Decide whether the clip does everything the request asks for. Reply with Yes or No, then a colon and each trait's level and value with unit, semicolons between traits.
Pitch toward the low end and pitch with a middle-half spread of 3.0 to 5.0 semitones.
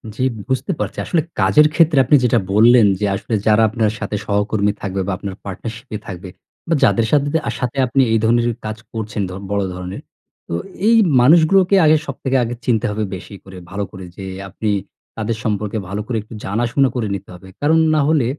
Yes: low, 110 Hz; average, 4.4 semitones